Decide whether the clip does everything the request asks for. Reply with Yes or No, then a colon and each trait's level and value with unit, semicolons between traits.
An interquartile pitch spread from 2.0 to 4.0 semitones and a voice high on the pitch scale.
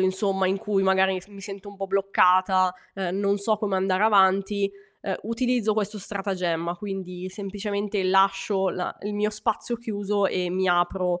No: narrow, 1.6 semitones; high, 195 Hz